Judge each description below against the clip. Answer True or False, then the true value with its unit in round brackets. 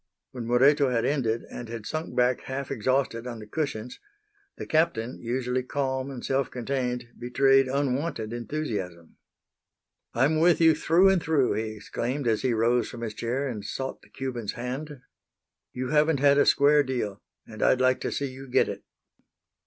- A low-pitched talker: True (130 Hz)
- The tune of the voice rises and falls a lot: False (3.1 semitones)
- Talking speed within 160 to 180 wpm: True (170 wpm)